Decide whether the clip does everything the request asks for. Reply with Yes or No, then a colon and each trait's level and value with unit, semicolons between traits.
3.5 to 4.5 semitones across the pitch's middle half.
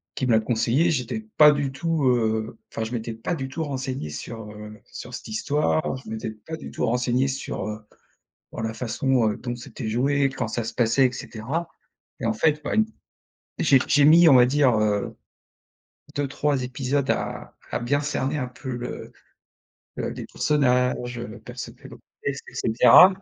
Yes: average, 3.9 semitones